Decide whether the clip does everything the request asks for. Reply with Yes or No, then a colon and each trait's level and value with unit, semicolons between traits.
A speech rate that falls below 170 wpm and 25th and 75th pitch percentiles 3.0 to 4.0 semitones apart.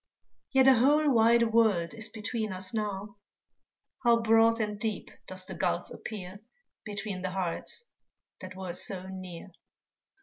Yes: average, 140 wpm; average, 3.4 semitones